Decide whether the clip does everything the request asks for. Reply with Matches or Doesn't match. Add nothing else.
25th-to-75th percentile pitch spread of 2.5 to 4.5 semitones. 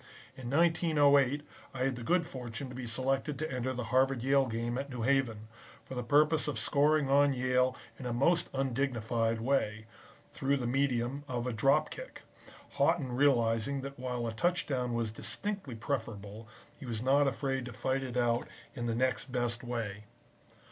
Matches